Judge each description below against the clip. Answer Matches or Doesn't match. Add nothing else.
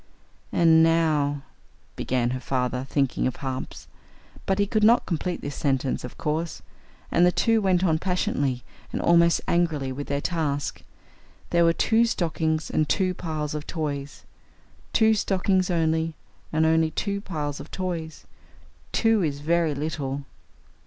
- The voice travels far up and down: Doesn't match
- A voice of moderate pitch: Matches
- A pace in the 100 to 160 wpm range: Matches